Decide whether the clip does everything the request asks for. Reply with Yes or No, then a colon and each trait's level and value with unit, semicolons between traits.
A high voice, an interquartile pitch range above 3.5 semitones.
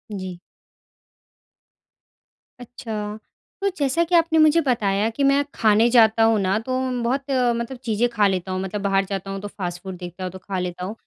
Yes: high, 215 Hz; average, 4.4 semitones